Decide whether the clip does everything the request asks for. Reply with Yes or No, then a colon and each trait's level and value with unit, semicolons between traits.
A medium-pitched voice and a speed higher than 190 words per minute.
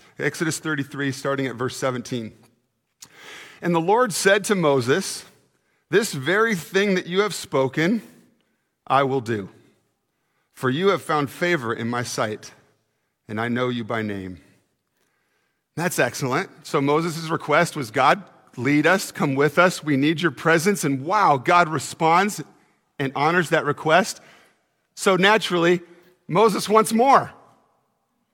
No: medium, 150 Hz; average, 140 wpm